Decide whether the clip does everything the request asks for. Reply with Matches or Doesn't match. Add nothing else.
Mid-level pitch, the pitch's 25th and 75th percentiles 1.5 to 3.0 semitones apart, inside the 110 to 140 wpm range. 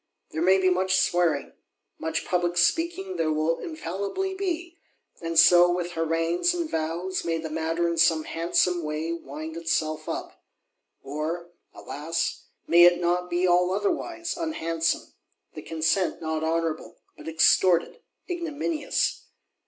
Matches